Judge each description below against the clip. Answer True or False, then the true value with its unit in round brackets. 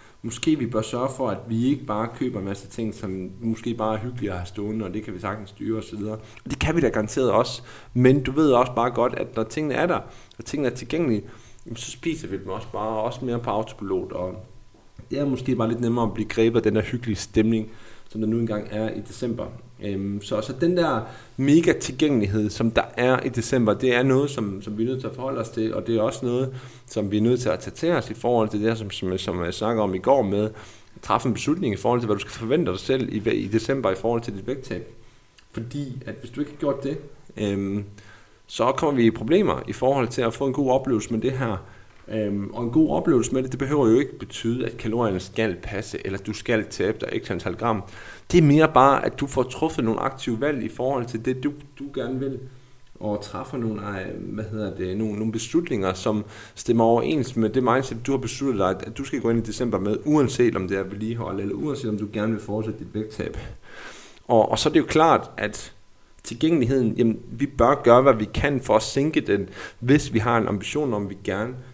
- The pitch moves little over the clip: False (3.3 semitones)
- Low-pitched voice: True (115 Hz)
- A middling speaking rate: False (245 wpm)